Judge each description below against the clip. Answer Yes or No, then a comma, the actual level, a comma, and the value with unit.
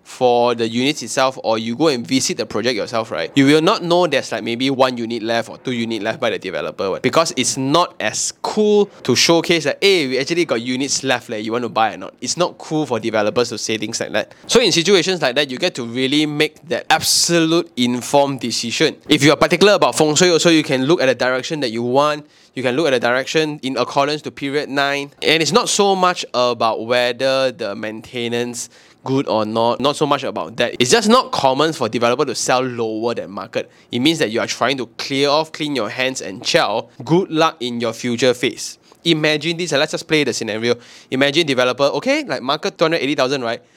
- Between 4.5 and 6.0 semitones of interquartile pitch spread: Yes, average, 4.9 semitones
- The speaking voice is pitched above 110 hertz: Yes, low, 135 Hz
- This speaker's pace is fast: Yes, fast, 230 wpm